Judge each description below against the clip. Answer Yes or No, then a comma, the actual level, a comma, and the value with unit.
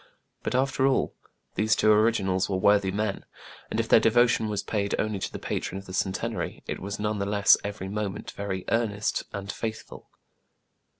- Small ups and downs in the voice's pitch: Yes, narrow, 1.7 semitones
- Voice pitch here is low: Yes, low, 105 Hz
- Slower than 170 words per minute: No, average, 180 wpm